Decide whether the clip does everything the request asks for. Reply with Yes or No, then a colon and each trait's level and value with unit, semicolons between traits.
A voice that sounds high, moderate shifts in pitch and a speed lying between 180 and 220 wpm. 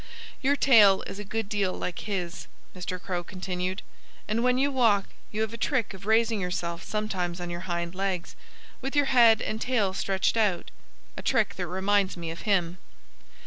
Yes: high, 195 Hz; average, 3.6 semitones; average, 185 wpm